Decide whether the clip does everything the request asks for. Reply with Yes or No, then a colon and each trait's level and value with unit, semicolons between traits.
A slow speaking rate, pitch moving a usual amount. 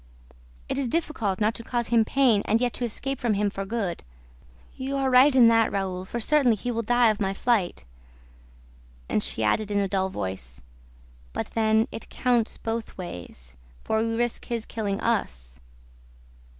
No: average, 175 wpm; average, 3.6 semitones